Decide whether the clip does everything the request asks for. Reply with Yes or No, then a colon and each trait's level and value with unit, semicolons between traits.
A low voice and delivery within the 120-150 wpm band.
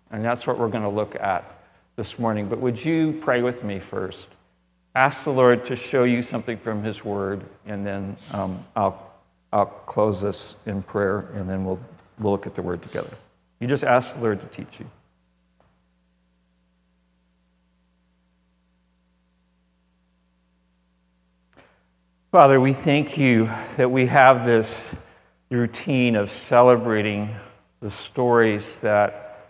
Yes: low, 105 Hz; slow, 135 wpm